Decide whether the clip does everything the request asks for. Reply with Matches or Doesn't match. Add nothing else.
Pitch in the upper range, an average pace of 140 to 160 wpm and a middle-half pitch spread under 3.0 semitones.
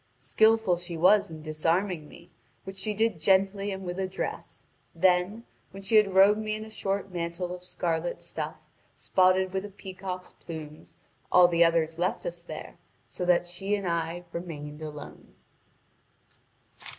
Doesn't match